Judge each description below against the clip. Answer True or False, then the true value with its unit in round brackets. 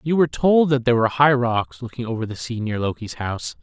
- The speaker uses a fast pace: True (250 wpm)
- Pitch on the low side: True (120 Hz)